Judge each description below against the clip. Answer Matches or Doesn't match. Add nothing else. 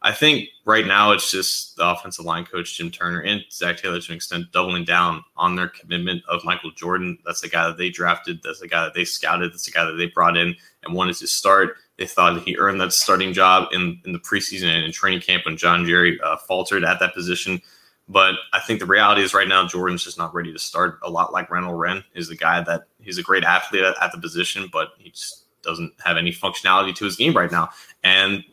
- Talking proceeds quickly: Matches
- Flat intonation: Matches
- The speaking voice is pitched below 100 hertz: Matches